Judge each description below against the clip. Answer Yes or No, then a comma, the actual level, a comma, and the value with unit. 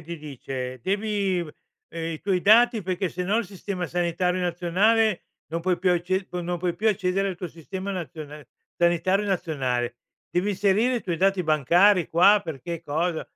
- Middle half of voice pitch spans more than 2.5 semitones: Yes, average, 2.9 semitones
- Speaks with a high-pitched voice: No, medium, 180 Hz